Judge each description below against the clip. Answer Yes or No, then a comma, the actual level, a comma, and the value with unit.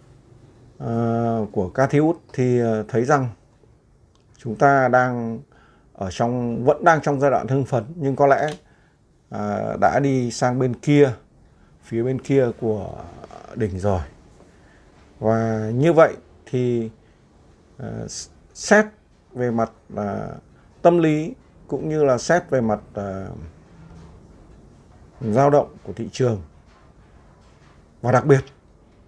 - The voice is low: Yes, low, 120 Hz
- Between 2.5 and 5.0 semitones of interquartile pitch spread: Yes, average, 4.2 semitones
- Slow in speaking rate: Yes, slow, 125 wpm